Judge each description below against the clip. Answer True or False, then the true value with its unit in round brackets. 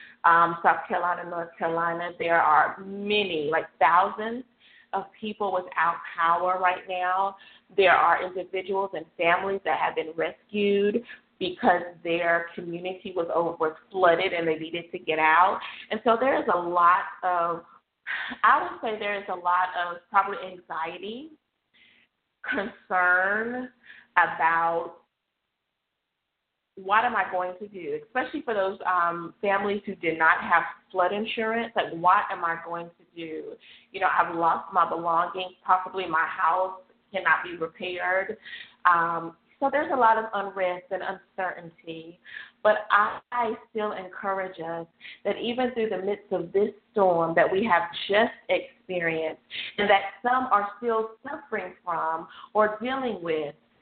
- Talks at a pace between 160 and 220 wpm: False (145 wpm)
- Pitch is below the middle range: False (185 Hz)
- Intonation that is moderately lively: True (3.5 semitones)